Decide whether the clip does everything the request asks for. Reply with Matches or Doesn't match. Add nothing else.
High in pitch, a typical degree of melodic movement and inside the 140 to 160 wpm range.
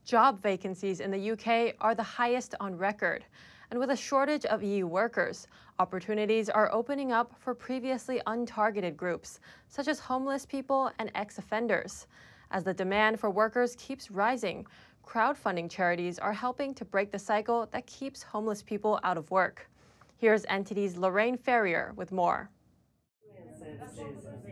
Matches